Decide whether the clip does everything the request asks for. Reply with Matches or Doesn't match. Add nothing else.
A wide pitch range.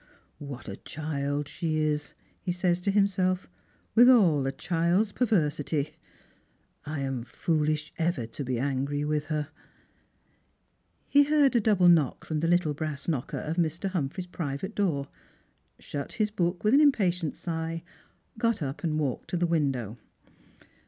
Doesn't match